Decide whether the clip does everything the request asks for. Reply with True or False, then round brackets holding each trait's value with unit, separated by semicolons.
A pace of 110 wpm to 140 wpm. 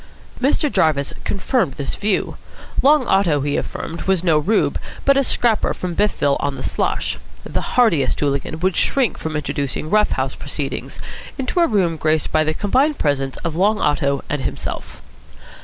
False (165 wpm)